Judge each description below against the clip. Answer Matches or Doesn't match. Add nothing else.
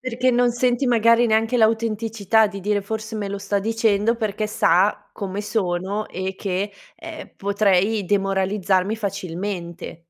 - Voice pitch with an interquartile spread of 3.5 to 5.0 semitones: Doesn't match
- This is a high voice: Matches